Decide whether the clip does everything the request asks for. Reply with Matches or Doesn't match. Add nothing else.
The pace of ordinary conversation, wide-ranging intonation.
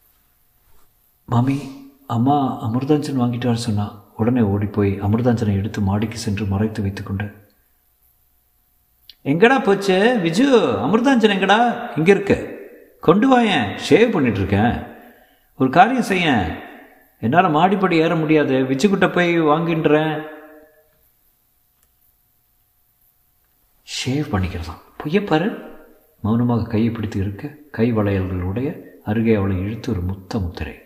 Matches